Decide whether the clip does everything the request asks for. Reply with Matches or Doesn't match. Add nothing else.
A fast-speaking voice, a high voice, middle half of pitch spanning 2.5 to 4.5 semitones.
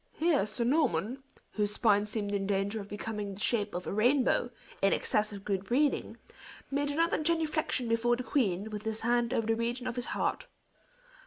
Doesn't match